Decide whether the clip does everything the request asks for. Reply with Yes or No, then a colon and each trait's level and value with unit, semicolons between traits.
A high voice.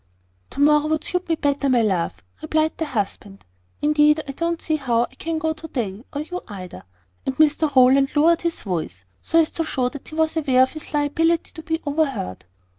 Yes: very high, 295 Hz